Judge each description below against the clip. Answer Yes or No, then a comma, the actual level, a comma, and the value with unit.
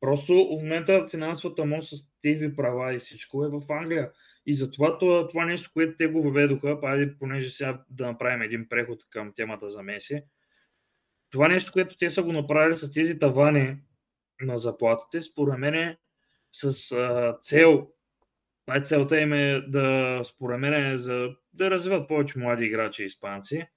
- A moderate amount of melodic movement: Yes, average, 3.8 semitones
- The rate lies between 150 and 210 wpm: Yes, fast, 165 wpm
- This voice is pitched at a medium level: Yes, medium, 145 Hz